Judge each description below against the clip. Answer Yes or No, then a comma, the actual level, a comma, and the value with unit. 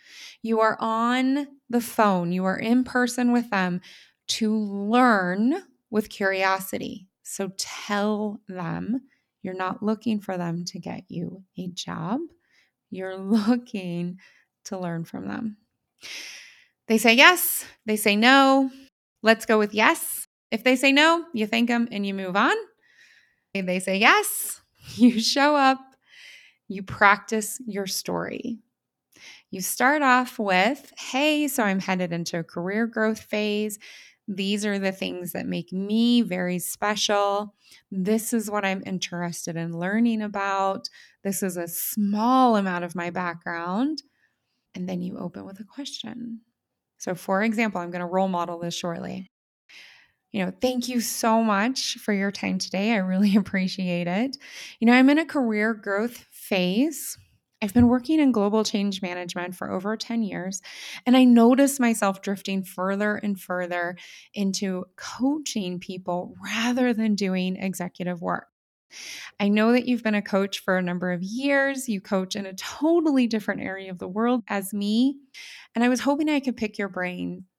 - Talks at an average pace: Yes, average, 155 wpm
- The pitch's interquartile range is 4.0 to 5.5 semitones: Yes, average, 4.4 semitones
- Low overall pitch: No, high, 210 Hz